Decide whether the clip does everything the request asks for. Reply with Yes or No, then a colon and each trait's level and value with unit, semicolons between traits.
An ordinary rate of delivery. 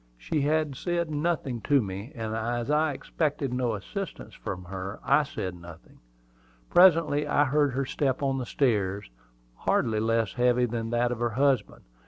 Yes: average, 160 wpm